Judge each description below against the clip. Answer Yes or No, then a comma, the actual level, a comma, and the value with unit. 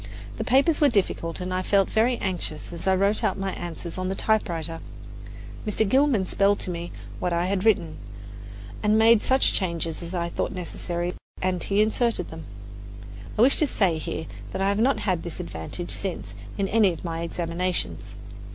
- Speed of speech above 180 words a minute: Yes, average, 190 wpm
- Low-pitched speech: No, medium, 185 Hz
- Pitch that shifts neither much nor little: Yes, average, 3.8 semitones